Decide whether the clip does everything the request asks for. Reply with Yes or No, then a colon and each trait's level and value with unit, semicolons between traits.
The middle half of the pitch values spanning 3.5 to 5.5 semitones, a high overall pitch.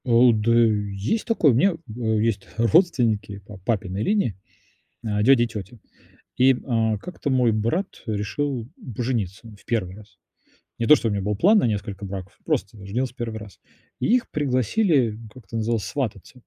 No: average, 3.9 semitones; low, 115 Hz